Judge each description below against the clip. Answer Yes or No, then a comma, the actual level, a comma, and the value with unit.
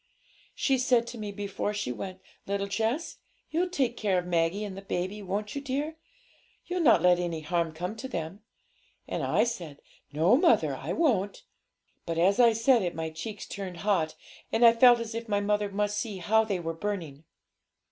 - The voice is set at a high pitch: Yes, high, 205 Hz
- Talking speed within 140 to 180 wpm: No, average, 190 wpm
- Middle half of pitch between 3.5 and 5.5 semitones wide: Yes, average, 4.6 semitones